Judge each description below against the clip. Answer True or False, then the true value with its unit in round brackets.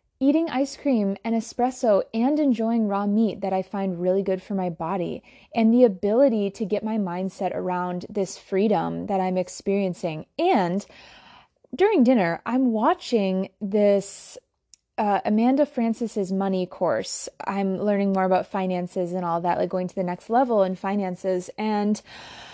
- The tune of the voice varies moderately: True (3.7 semitones)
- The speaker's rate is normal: True (155 wpm)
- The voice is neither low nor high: False (200 Hz)